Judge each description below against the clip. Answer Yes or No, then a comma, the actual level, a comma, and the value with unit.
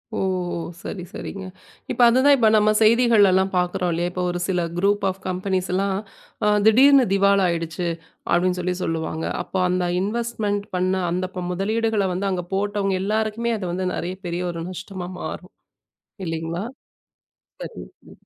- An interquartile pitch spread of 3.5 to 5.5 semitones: No, average, 2.9 semitones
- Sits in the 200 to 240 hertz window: No, high, 190 Hz